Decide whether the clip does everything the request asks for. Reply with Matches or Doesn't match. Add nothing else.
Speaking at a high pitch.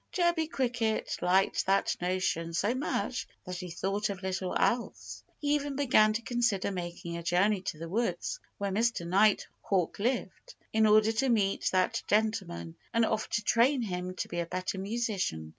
Matches